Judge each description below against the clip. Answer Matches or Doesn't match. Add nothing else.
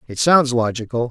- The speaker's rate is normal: Matches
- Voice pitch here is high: Doesn't match